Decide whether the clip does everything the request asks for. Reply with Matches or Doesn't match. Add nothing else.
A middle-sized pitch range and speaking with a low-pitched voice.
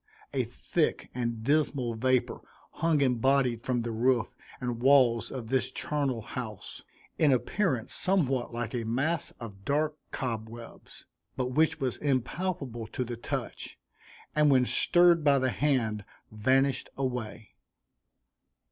Matches